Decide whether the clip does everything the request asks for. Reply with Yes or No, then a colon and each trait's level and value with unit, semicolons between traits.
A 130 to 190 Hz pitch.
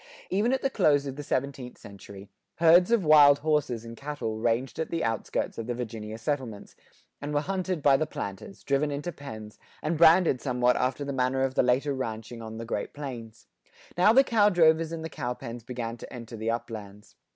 Yes: low, 135 Hz